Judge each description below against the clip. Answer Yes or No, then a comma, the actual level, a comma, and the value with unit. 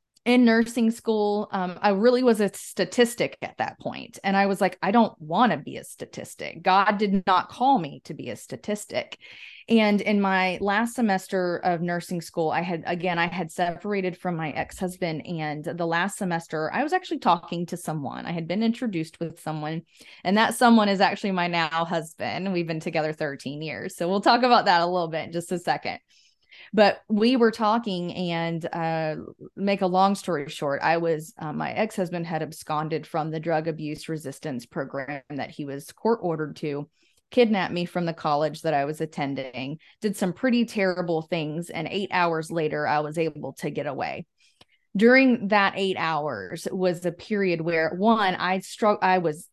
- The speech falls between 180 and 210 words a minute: Yes, average, 190 wpm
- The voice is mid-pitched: Yes, medium, 175 Hz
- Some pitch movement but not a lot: Yes, average, 4.0 semitones